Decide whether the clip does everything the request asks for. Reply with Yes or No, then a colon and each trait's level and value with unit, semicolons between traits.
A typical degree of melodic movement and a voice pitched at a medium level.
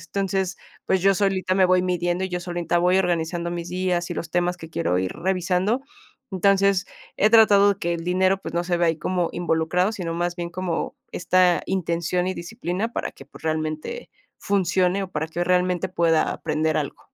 No: narrow, 1.7 semitones; medium, 180 Hz